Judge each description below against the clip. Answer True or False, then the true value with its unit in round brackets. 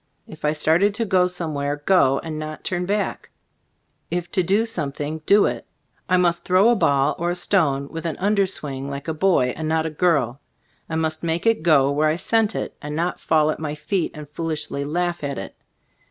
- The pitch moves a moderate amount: True (3.4 semitones)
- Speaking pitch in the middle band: True (160 Hz)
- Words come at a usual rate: False (210 wpm)